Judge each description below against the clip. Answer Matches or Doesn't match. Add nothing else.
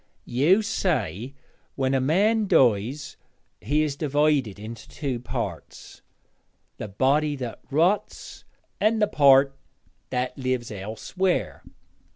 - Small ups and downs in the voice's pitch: Doesn't match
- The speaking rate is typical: Doesn't match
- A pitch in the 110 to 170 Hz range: Matches